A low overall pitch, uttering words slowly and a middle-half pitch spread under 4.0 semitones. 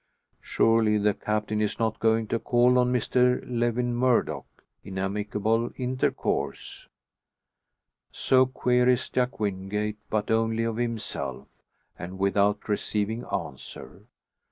Yes: low, 110 Hz; slow, 110 wpm; average, 2.8 semitones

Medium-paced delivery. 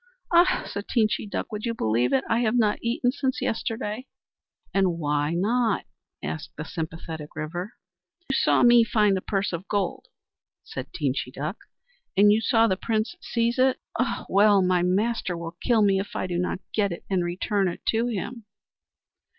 Yes: average, 175 wpm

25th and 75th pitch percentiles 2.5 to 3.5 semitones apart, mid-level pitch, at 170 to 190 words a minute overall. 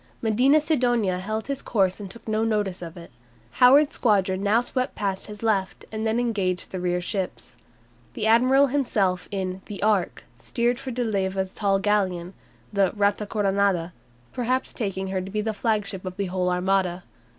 No: average, 3.2 semitones; high, 200 Hz; average, 175 wpm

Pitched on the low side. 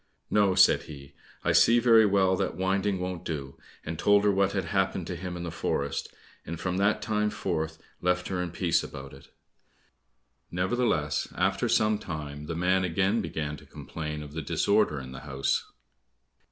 Yes: very low, 90 Hz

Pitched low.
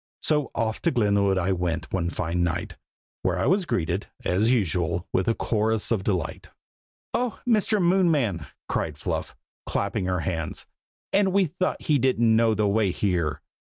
Yes: low, 105 Hz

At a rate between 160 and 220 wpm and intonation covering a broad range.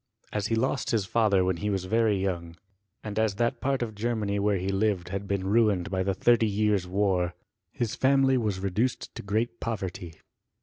No: average, 190 wpm; average, 3.0 semitones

